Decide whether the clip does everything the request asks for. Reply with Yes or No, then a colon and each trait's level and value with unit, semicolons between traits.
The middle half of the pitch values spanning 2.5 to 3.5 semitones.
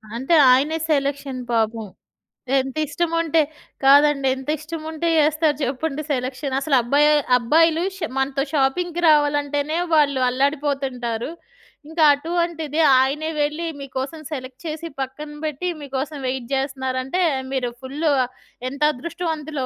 Yes: average, 2.9 semitones